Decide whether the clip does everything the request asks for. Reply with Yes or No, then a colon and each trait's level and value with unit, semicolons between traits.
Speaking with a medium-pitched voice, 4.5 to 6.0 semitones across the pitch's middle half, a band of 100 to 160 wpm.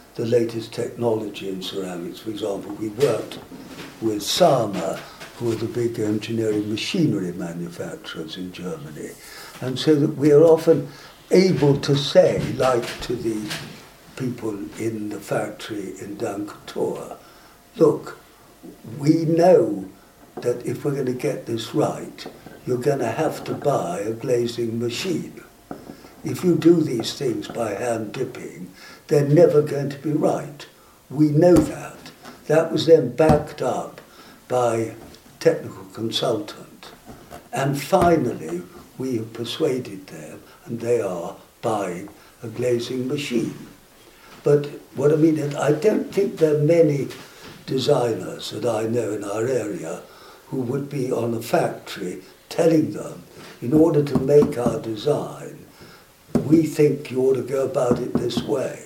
No: low, 130 Hz; average, 4.9 semitones; average, 140 wpm